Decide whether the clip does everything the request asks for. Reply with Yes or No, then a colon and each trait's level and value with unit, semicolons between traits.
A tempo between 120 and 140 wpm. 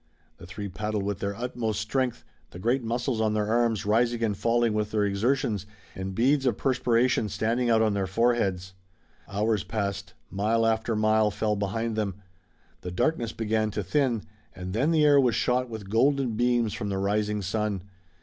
No: average, 180 wpm